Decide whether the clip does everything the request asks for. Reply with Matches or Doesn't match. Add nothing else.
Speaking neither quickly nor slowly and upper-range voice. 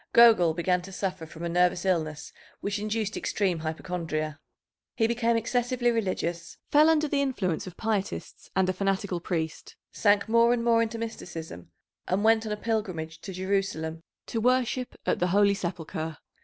Matches